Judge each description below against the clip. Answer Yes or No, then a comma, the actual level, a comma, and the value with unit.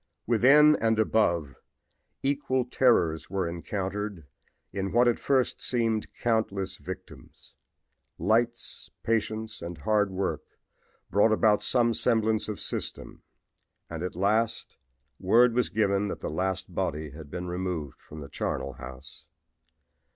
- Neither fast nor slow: No, slow, 125 wpm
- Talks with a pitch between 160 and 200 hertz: No, low, 105 Hz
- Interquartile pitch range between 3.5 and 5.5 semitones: Yes, average, 4.6 semitones